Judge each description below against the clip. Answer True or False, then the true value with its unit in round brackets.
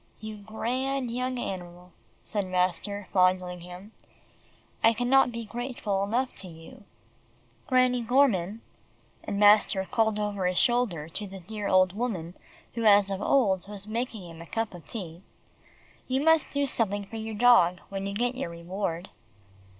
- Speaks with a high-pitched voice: True (205 Hz)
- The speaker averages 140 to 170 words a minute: True (160 wpm)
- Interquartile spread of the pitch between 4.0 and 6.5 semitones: True (4.6 semitones)